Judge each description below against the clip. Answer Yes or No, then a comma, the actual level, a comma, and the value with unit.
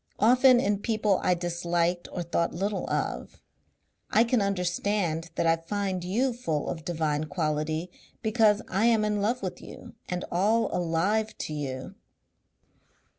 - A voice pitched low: No, medium, 185 Hz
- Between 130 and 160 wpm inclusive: Yes, average, 145 wpm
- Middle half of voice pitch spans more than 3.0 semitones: Yes, average, 4.2 semitones